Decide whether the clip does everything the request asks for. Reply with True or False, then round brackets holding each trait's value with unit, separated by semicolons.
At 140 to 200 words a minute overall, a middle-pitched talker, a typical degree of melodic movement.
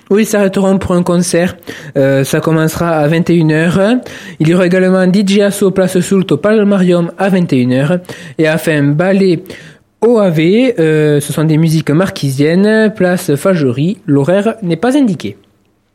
True (145 wpm; 175 Hz; 4.0 semitones)